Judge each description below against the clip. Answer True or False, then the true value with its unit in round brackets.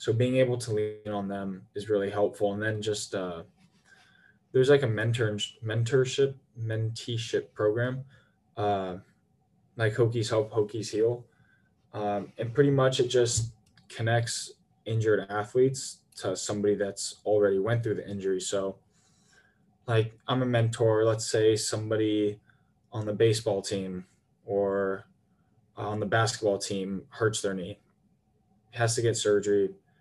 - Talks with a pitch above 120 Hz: False (110 Hz)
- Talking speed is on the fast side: False (135 wpm)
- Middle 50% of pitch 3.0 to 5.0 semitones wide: False (2.4 semitones)